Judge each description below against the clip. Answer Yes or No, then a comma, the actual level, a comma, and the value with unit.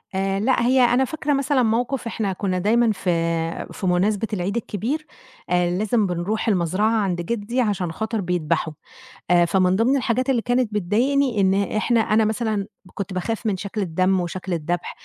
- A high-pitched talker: Yes, high, 205 Hz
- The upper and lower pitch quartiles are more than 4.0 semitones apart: Yes, average, 4.5 semitones